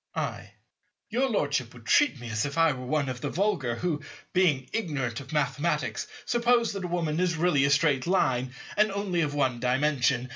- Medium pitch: Yes, medium, 150 Hz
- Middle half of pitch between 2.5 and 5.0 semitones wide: No, wide, 5.6 semitones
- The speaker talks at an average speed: Yes, average, 190 wpm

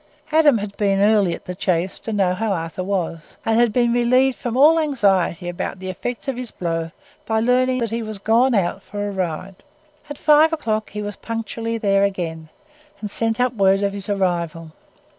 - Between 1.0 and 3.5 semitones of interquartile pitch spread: No, average, 4.1 semitones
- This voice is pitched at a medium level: No, high, 205 Hz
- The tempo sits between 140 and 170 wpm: No, average, 200 wpm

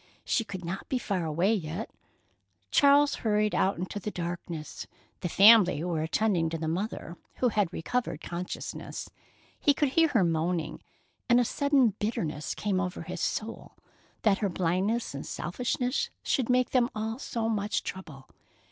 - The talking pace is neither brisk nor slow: Yes, average, 155 wpm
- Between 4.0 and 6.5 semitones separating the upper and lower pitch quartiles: Yes, average, 5.2 semitones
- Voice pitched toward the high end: Yes, high, 200 Hz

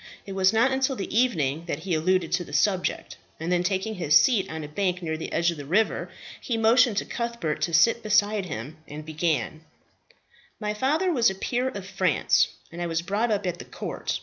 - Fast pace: Yes, fast, 215 wpm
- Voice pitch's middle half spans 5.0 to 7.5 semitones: Yes, wide, 5.4 semitones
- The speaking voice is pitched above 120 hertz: Yes, high, 190 Hz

